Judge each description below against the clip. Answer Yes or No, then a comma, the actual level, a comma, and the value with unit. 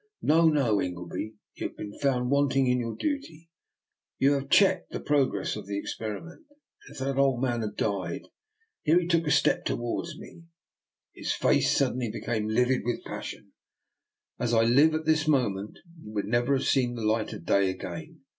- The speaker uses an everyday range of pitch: No, wide, 6.0 semitones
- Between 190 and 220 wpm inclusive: Yes, average, 200 wpm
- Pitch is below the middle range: Yes, low, 125 Hz